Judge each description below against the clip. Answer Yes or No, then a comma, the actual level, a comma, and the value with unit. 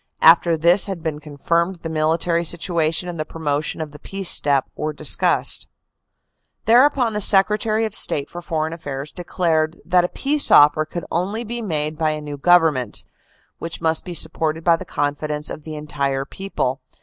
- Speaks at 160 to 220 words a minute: Yes, average, 180 wpm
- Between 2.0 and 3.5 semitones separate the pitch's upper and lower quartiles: Yes, average, 2.8 semitones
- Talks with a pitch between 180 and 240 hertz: No, medium, 160 Hz